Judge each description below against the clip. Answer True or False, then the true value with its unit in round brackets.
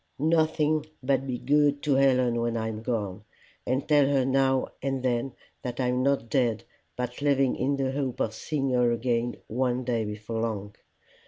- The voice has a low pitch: True (130 Hz)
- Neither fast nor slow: True (175 wpm)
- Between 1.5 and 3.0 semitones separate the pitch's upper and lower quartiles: True (2.7 semitones)